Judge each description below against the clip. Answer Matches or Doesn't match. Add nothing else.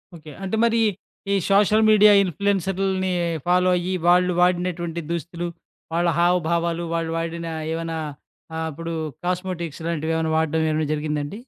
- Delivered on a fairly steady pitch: Matches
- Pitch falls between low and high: Matches